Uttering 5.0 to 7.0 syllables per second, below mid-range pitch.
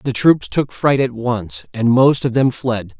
No: 4.0 syllables/s; low, 125 Hz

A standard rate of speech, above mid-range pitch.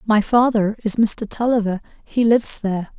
Yes: average, 160 wpm; high, 220 Hz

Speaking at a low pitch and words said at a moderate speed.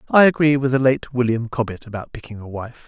No: low, 125 Hz; fast, 230 wpm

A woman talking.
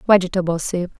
Yes: female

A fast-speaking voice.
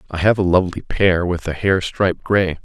Yes: fast, 225 wpm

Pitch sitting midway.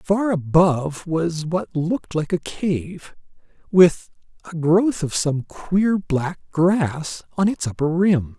Yes: medium, 165 Hz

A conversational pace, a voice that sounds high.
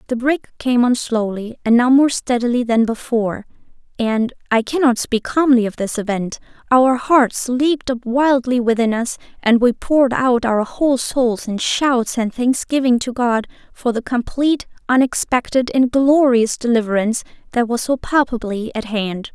Yes: average, 155 wpm; high, 245 Hz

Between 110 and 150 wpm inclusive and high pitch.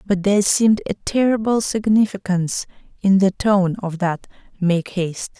Yes: average, 145 wpm; high, 195 Hz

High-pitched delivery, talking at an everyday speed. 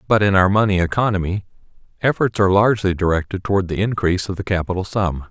No: very low, 95 Hz; average, 180 wpm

